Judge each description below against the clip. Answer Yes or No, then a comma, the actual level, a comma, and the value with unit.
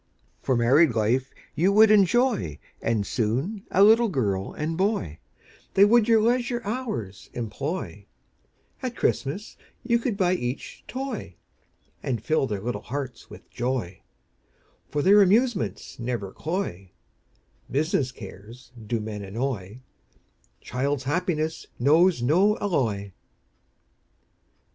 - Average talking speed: No, slow, 115 wpm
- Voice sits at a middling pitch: Yes, medium, 145 Hz